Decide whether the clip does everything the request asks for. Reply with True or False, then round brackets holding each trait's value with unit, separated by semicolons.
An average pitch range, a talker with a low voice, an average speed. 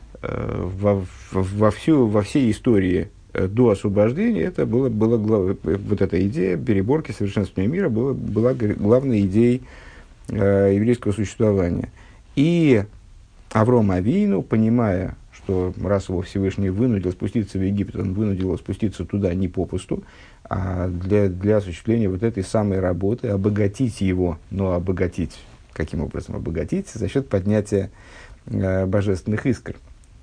True (3.2 semitones; 100 Hz; 125 wpm)